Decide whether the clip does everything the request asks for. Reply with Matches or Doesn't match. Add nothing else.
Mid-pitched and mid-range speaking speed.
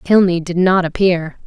Matches